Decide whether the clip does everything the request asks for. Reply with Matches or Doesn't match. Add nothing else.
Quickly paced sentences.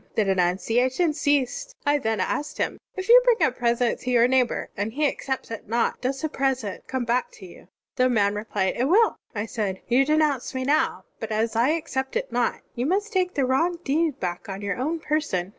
Matches